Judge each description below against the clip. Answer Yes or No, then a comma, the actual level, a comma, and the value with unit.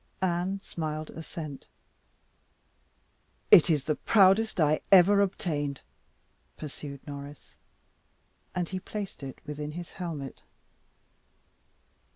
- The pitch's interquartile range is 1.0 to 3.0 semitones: No, average, 4.1 semitones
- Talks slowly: Yes, slow, 95 wpm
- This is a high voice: No, medium, 160 Hz